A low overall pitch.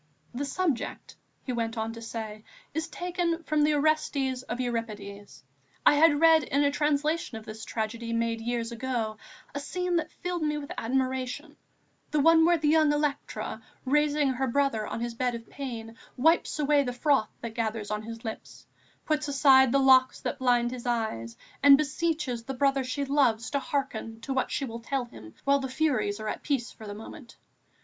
No: very high, 260 Hz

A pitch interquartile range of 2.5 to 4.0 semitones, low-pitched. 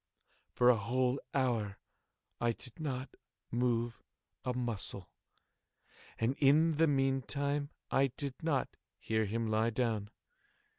Yes: average, 3.2 semitones; low, 125 Hz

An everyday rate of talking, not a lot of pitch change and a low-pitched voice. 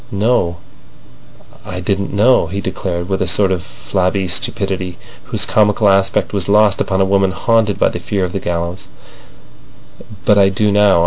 Yes: average, 170 wpm; narrow, 1.9 semitones; very low, 95 Hz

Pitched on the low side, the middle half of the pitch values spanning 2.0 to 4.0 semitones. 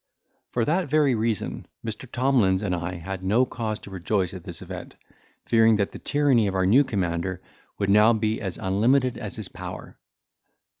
No: low, 105 Hz; average, 4.4 semitones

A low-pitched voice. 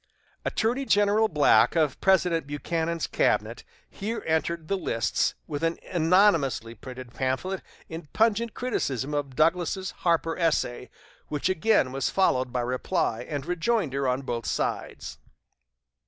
No: medium, 165 Hz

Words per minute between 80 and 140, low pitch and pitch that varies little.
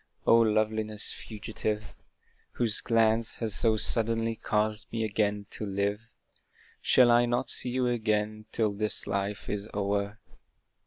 Yes: slow, 135 wpm; low, 110 Hz; narrow, 1.5 semitones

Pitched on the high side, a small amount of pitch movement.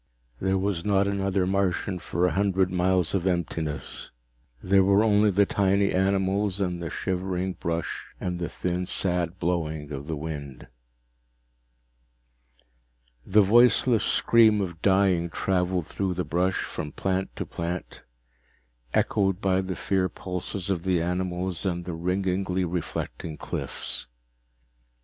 No: very low, 95 Hz; narrow, 2.0 semitones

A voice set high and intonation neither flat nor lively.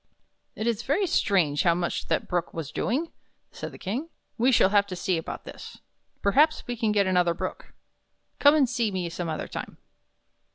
No: high, 200 Hz; wide, 6.1 semitones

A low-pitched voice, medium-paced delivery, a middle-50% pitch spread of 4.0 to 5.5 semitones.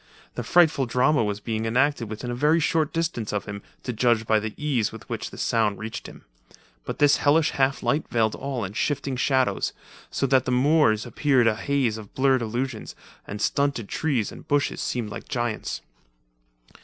Yes: low, 125 Hz; average, 185 wpm; average, 4.3 semitones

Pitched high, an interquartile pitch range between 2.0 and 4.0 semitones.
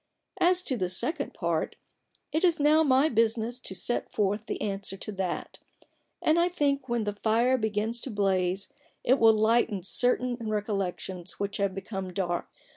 No: high, 220 Hz; average, 4.7 semitones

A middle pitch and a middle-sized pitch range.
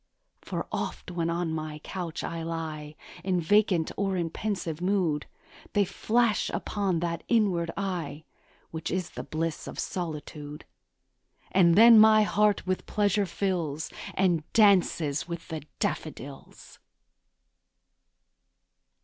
Yes: medium, 175 Hz; average, 3.7 semitones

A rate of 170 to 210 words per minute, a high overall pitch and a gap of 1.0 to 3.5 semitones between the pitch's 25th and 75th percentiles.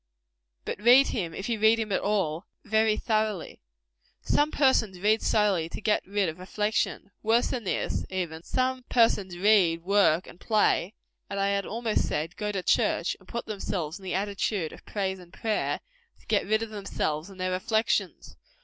Yes: average, 180 wpm; high, 205 Hz; average, 3.0 semitones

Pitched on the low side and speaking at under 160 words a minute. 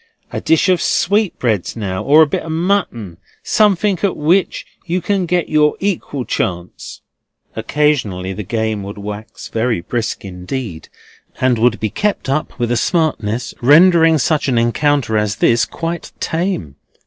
Yes: low, 130 Hz; average, 150 wpm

